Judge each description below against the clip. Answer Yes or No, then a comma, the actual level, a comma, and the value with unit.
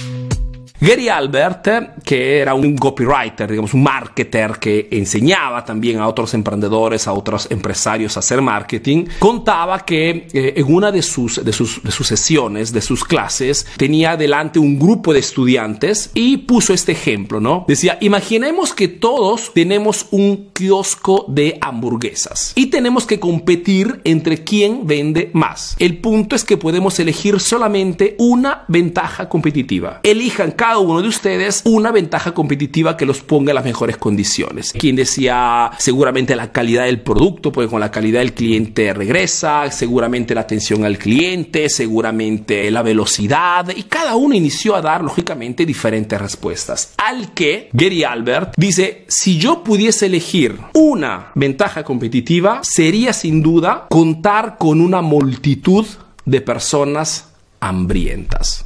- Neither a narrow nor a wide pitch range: No, wide, 8.3 semitones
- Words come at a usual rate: Yes, average, 145 wpm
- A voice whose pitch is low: No, medium, 155 Hz